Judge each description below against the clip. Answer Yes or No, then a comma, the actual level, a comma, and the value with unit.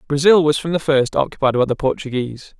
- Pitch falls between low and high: Yes, medium, 145 Hz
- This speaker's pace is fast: Yes, fast, 210 wpm